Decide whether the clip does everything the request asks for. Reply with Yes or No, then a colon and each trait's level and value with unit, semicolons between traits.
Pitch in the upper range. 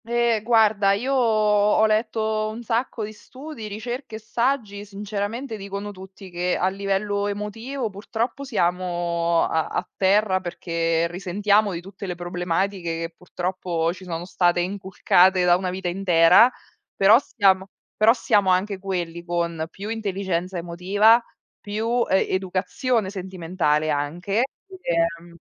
Yes: high, 195 Hz